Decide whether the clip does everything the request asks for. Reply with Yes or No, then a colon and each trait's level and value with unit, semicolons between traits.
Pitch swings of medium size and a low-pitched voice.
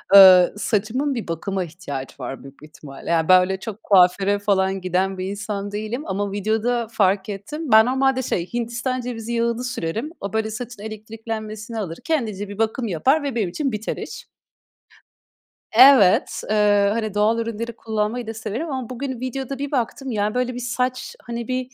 No: average, 3.7 semitones; high, 220 Hz